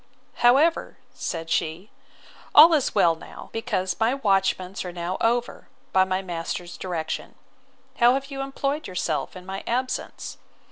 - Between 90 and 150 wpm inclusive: Yes, average, 140 wpm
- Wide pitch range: Yes, wide, 6.3 semitones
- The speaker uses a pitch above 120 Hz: Yes, high, 190 Hz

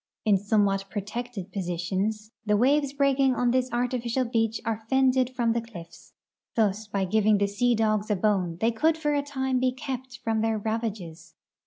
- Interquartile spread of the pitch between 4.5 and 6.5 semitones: No, average, 3.8 semitones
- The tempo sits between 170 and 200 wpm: Yes, average, 175 wpm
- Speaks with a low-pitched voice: No, high, 225 Hz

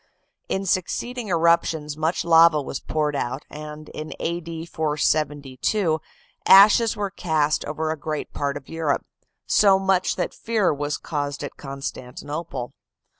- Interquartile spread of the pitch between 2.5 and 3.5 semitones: Yes, average, 2.8 semitones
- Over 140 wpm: No, slow, 135 wpm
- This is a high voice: No, medium, 155 Hz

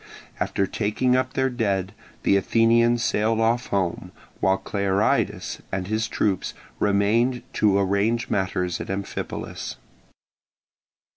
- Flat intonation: No, average, 3.1 semitones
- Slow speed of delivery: Yes, slow, 115 wpm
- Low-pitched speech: Yes, low, 105 Hz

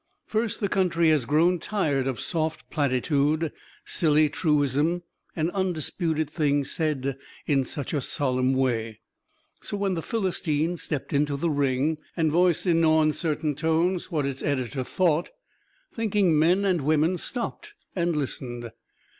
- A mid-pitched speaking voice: Yes, medium, 155 Hz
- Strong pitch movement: No, average, 3.6 semitones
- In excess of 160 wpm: No, average, 140 wpm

